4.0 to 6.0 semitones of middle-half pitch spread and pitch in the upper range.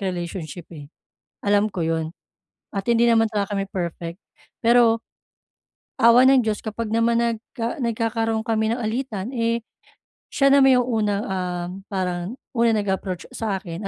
No: average, 3.6 semitones; high, 220 Hz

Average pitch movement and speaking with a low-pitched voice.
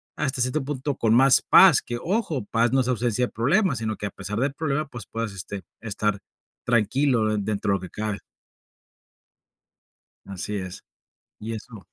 Yes: average, 4.2 semitones; low, 120 Hz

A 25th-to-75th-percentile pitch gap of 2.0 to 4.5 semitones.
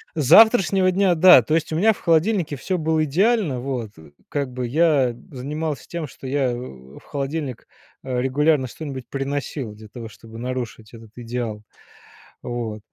No: average, 4.9 semitones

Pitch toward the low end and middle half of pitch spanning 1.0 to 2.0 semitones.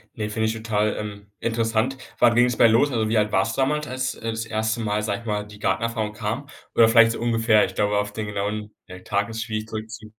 Yes: low, 110 Hz; narrow, 1.5 semitones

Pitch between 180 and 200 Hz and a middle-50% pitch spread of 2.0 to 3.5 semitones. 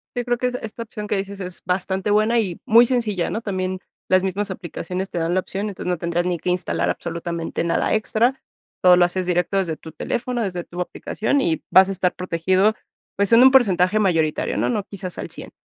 Yes: high, 190 Hz; average, 3.2 semitones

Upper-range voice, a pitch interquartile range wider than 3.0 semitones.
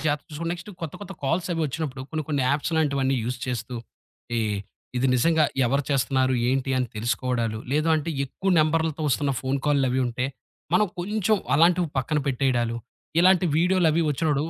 No: medium, 145 Hz; average, 4.0 semitones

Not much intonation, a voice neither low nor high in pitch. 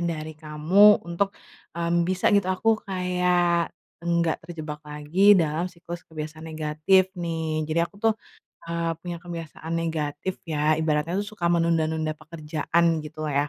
Yes: narrow, 2.3 semitones; medium, 165 Hz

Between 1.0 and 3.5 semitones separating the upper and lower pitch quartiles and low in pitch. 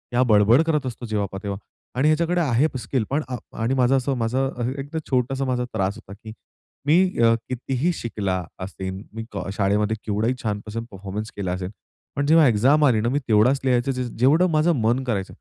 No: average, 4.5 semitones; low, 120 Hz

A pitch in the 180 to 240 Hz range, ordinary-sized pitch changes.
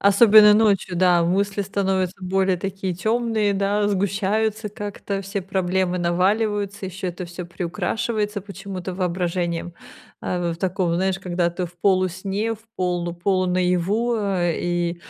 No: high, 190 Hz; narrow, 2.3 semitones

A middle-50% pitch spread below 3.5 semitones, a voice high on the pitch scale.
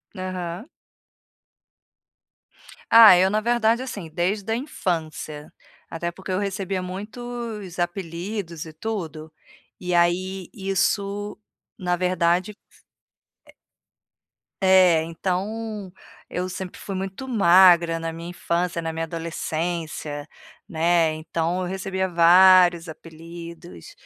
No: narrow, 2.6 semitones; medium, 180 Hz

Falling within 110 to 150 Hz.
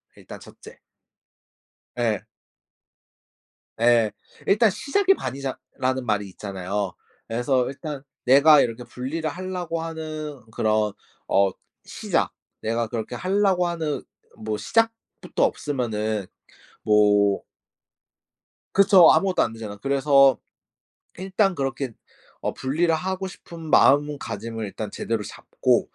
Yes: low, 135 Hz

